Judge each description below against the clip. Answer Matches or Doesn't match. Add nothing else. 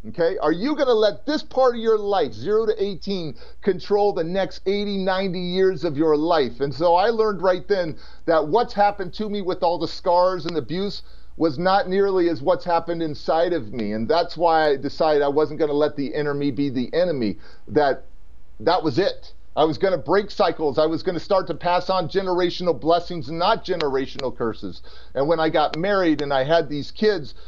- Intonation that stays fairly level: Doesn't match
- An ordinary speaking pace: Doesn't match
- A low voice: Doesn't match